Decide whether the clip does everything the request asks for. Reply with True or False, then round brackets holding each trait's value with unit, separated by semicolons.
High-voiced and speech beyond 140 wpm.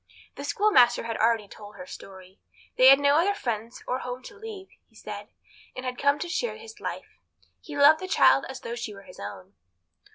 True (255 Hz; 205 wpm)